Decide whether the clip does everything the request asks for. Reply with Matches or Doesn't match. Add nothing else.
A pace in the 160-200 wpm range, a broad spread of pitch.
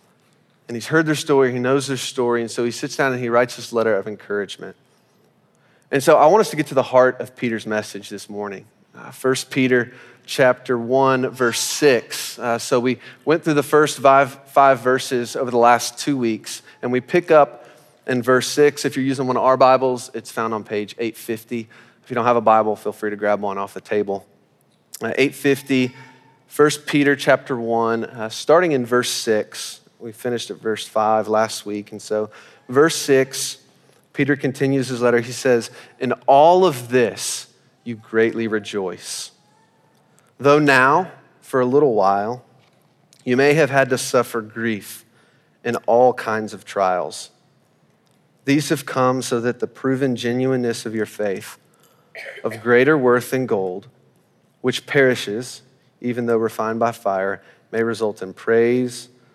Doesn't match